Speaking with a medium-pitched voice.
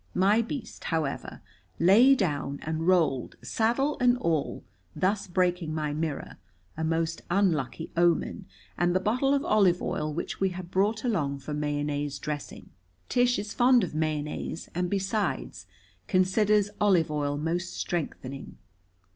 Yes: medium, 175 Hz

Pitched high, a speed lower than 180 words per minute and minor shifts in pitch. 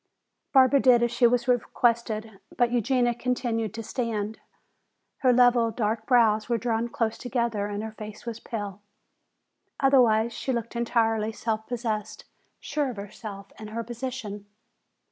Yes: high, 230 Hz; average, 145 wpm; narrow, 2.1 semitones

